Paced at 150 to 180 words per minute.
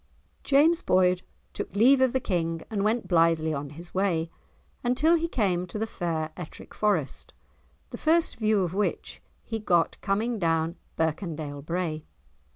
Yes: average, 155 wpm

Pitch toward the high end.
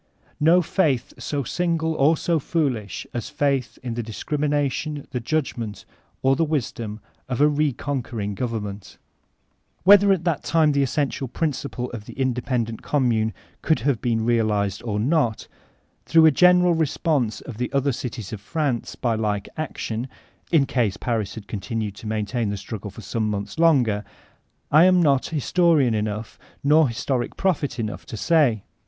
No: low, 125 Hz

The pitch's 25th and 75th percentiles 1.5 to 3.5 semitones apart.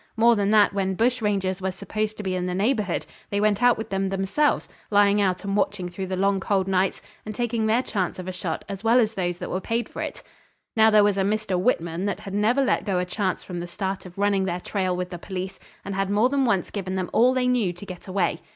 Yes: narrow, 2.5 semitones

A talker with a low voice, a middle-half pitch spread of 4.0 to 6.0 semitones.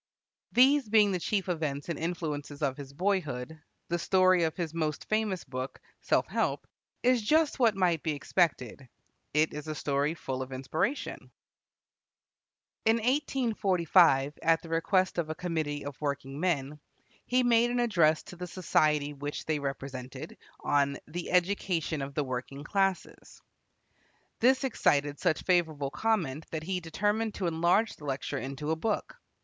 No: medium, 160 Hz; average, 5.1 semitones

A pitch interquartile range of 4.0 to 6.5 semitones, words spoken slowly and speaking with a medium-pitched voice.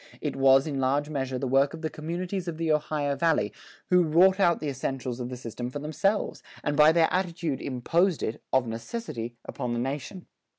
No: average, 4.4 semitones; average, 200 wpm; medium, 145 Hz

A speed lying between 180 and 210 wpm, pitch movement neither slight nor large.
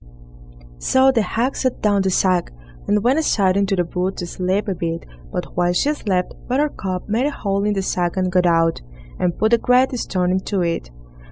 Yes: average, 200 wpm; average, 3.9 semitones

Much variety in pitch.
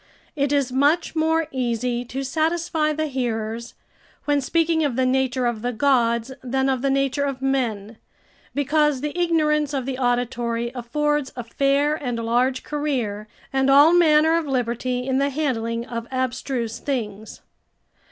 No: average, 3.6 semitones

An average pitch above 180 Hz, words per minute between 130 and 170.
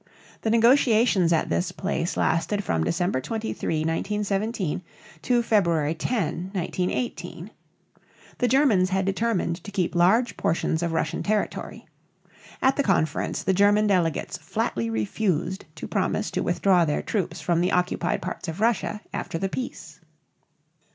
Yes: high, 190 Hz; average, 140 wpm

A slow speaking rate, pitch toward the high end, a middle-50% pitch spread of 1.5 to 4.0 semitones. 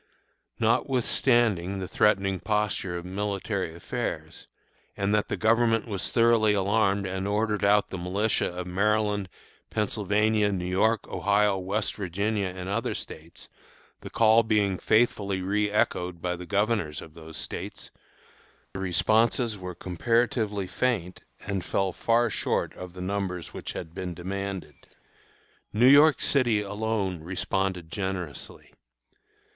No: slow, 130 wpm; low, 100 Hz; average, 2.9 semitones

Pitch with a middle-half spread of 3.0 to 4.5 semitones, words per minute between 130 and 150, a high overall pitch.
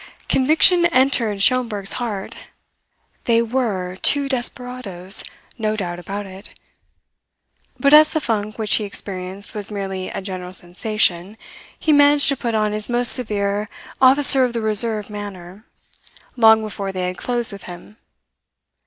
Yes: average, 4.2 semitones; average, 140 wpm; high, 215 Hz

